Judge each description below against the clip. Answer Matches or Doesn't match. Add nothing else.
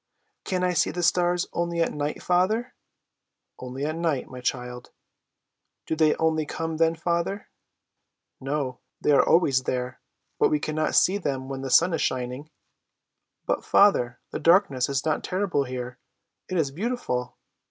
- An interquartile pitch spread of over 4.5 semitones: Matches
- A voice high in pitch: Doesn't match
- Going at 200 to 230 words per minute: Doesn't match